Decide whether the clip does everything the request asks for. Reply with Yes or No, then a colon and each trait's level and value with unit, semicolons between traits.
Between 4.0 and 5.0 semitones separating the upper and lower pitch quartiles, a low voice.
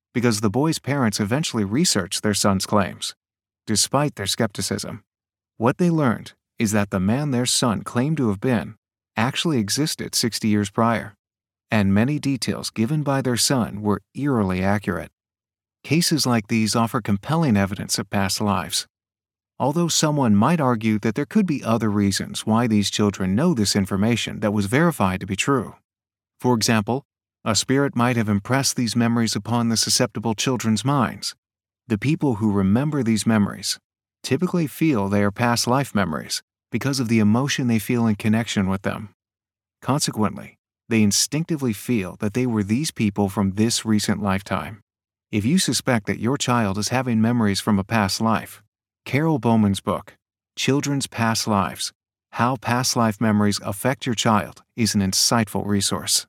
No: average, 3.5 semitones; low, 110 Hz